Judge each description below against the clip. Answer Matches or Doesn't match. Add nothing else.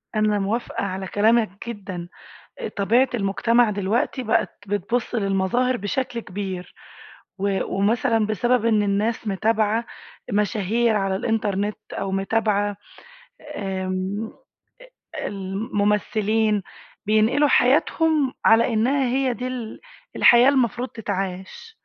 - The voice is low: Doesn't match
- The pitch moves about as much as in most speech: Matches